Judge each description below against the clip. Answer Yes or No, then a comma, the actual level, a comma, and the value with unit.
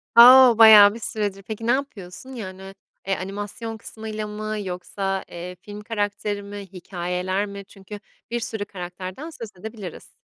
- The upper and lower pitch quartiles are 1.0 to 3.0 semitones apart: Yes, narrow, 2.4 semitones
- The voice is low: No, high, 205 Hz